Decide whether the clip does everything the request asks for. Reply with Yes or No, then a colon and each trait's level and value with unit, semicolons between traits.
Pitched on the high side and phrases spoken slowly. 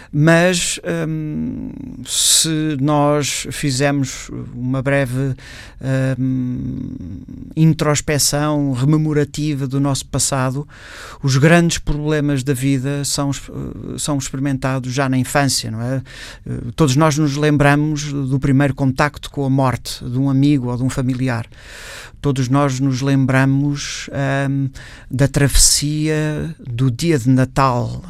No: medium, 140 Hz; slow, 115 wpm